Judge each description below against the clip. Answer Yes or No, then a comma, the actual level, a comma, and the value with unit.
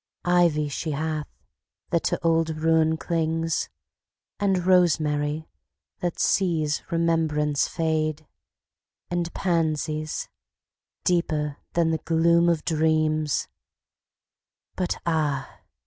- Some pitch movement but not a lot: No, narrow, 1.6 semitones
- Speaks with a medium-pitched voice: Yes, medium, 160 Hz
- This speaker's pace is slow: Yes, slow, 90 wpm